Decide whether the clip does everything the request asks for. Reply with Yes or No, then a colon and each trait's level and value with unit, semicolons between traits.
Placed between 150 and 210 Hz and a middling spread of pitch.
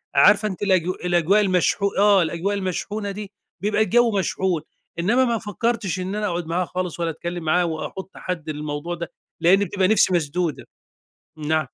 Yes: medium, 185 Hz; average, 3.2 semitones